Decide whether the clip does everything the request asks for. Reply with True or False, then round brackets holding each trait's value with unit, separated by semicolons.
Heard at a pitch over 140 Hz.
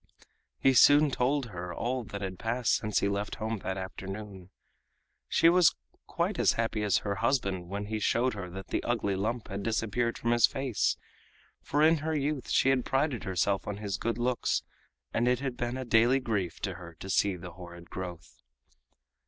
False (110 Hz)